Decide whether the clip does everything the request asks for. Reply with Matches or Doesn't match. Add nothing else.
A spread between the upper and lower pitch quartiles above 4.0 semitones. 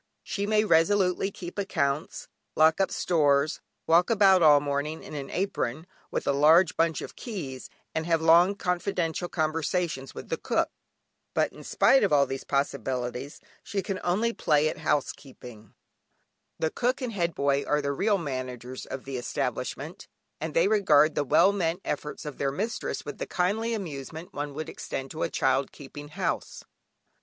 Matches